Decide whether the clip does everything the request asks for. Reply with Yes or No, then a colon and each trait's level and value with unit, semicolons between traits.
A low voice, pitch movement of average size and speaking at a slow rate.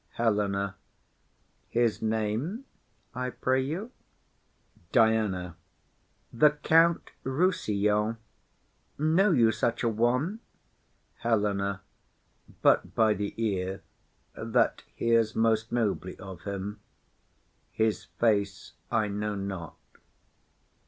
Yes: low, 110 Hz; average, 3.3 semitones; slow, 90 wpm